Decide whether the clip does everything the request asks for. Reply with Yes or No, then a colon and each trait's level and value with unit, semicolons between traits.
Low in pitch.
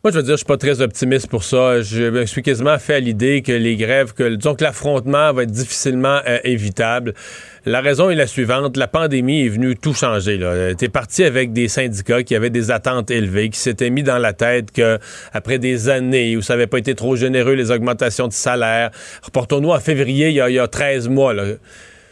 Yes: low, 125 Hz